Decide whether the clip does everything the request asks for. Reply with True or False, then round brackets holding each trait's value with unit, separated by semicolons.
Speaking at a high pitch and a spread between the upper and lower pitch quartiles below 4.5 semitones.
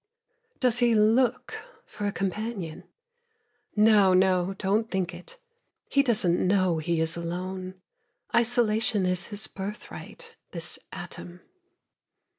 True (195 Hz; 3.6 semitones)